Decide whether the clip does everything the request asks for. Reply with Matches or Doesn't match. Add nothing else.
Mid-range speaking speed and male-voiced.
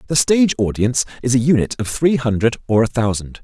Doesn't match